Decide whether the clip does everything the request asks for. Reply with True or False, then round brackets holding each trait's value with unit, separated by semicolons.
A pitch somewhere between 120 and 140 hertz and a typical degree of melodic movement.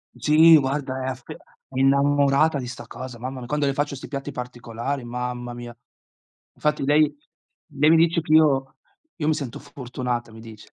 True (135 Hz; 3.1 semitones)